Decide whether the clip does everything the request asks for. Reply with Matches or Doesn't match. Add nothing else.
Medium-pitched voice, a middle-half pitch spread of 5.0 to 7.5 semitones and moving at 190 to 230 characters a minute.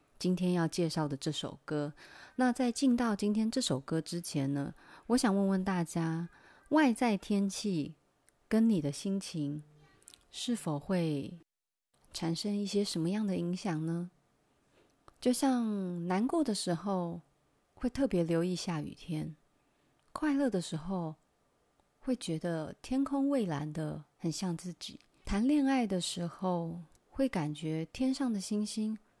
Matches